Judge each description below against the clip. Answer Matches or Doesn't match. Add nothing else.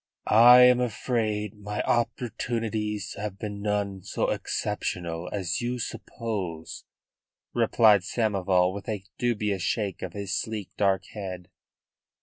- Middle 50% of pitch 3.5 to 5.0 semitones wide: Doesn't match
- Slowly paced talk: Matches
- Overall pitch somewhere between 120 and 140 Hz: Doesn't match